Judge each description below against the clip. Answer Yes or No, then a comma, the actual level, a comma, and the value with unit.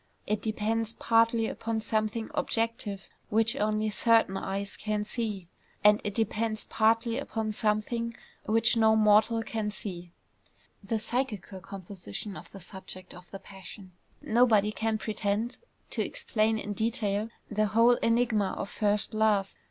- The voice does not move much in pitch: Yes, narrow, 1.8 semitones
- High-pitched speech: Yes, high, 215 Hz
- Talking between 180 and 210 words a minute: No, average, 140 wpm